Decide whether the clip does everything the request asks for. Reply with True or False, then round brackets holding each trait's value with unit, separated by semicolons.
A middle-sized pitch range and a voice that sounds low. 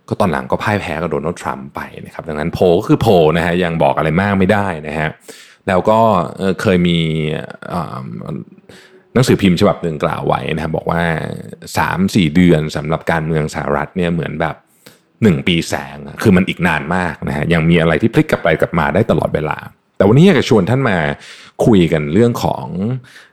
True (3.8 semitones; 85 Hz)